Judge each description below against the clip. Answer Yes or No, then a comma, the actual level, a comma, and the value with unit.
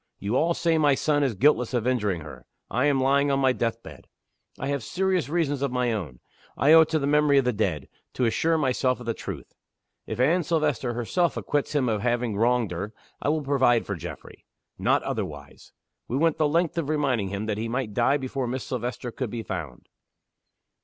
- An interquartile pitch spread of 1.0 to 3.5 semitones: No, average, 4.3 semitones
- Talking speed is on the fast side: Yes, fast, 210 wpm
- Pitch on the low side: Yes, low, 130 Hz